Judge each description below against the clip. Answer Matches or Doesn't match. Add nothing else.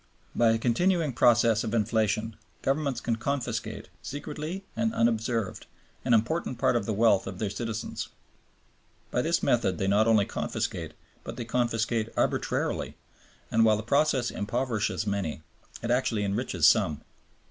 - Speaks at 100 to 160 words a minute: Matches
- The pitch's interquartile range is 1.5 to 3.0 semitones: Matches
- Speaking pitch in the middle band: Doesn't match